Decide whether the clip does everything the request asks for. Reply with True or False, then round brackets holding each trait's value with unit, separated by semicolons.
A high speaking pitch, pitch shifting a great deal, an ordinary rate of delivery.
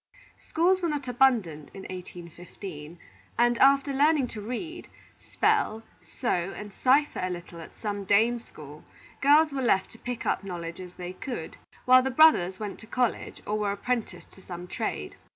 True (220 Hz; 6.6 semitones; 170 wpm)